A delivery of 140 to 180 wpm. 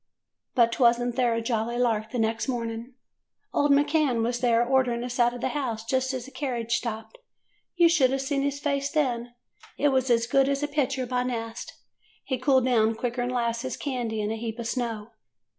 No: fast, 205 wpm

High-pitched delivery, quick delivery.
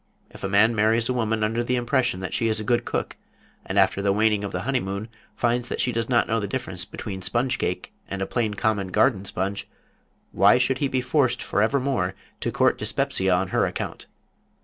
No: low, 110 Hz; fast, 210 wpm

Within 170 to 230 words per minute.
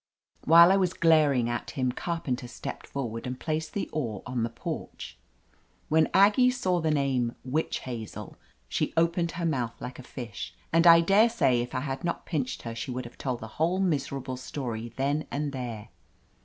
Yes: average, 185 wpm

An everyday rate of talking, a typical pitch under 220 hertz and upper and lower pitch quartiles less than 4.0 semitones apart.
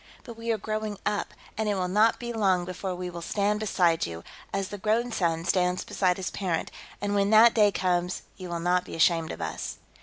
No: fast, 220 wpm; high, 190 Hz; average, 3.1 semitones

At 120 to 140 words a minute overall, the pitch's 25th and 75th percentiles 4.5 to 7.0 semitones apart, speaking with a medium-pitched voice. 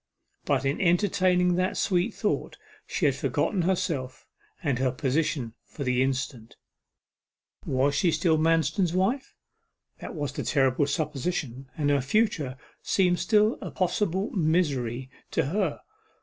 Yes: slow, 135 wpm; wide, 5.4 semitones; medium, 160 Hz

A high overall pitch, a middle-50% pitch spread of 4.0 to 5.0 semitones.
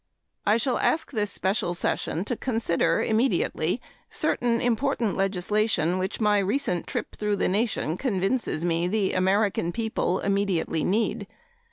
No: high, 205 Hz; average, 3.6 semitones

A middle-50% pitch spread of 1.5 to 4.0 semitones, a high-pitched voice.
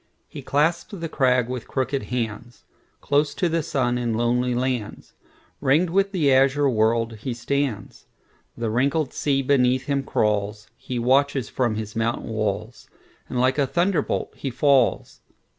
No: average, 3.4 semitones; low, 130 Hz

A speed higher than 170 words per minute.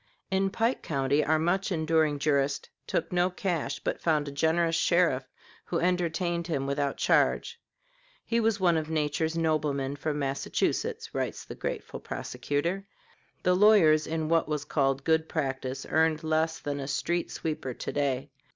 No: average, 155 wpm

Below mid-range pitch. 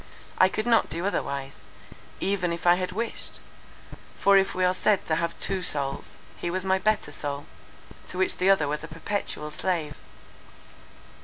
No: medium, 180 Hz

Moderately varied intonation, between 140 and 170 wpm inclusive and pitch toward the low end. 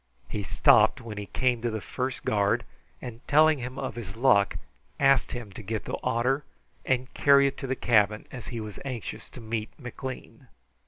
No: average, 3.4 semitones; average, 190 wpm; low, 120 Hz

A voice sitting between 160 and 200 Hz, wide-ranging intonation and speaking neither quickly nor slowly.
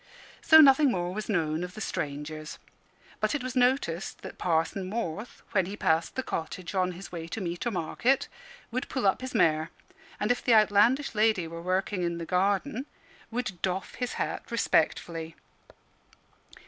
Yes: high, 190 Hz; wide, 6.0 semitones; average, 170 wpm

